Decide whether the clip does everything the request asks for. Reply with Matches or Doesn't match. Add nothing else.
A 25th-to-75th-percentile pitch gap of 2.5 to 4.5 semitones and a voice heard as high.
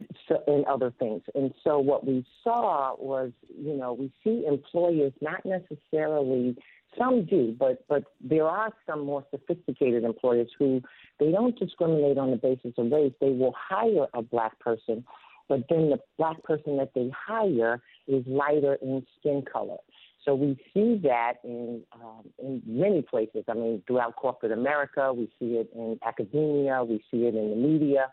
Doesn't match